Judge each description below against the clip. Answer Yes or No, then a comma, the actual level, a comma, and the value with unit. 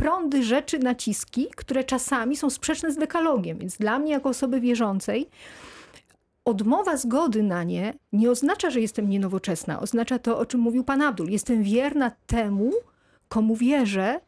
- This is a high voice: Yes, high, 245 Hz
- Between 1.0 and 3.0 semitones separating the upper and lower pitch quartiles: No, average, 4.4 semitones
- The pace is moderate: Yes, average, 150 wpm